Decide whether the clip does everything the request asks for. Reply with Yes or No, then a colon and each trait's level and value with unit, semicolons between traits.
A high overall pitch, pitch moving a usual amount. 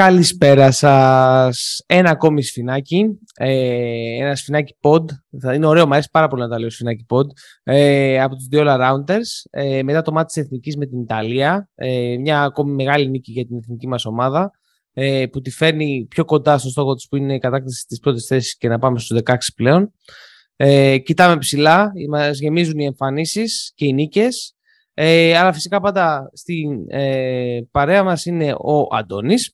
No: medium, 140 Hz; average, 3.7 semitones